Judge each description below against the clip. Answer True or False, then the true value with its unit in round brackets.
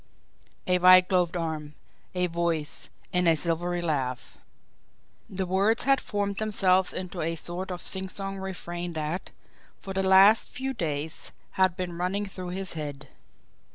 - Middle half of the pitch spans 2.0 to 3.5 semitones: True (2.4 semitones)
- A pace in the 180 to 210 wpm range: False (145 wpm)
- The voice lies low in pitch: False (180 Hz)